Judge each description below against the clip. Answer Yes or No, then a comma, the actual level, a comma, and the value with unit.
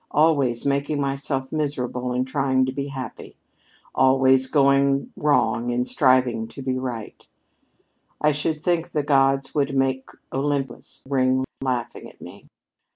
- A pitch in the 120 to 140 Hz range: Yes, low, 135 Hz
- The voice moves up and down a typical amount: No, narrow, 1.6 semitones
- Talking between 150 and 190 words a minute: No, slow, 135 wpm